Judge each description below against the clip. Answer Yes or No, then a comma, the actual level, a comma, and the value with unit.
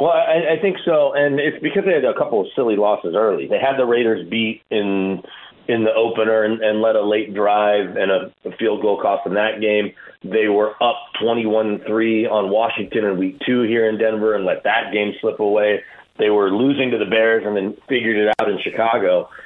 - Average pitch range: Yes, average, 4.3 semitones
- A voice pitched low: Yes, low, 110 Hz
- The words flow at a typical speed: No, fast, 225 wpm